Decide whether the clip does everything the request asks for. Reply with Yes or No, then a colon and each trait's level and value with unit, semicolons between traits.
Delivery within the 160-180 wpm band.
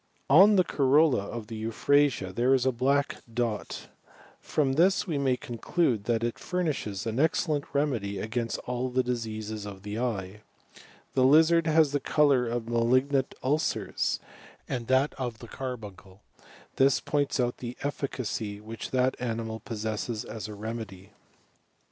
No: slow, 135 wpm